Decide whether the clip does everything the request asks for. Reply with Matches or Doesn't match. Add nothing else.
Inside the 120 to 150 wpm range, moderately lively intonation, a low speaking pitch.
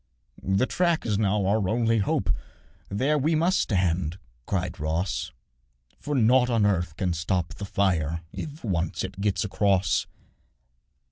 Matches